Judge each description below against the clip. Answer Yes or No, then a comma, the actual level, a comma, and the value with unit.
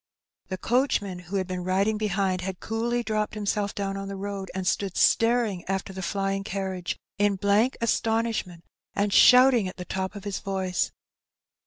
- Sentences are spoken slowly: No, average, 170 wpm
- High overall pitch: Yes, high, 195 Hz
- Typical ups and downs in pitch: No, narrow, 2.2 semitones